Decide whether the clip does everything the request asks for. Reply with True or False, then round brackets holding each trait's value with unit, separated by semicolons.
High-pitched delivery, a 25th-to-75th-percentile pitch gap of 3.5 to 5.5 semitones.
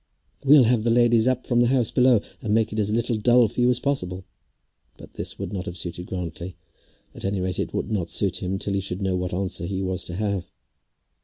False (100 Hz; 4.5 semitones)